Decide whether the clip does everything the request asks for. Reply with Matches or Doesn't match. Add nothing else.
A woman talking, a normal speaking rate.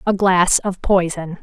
Matches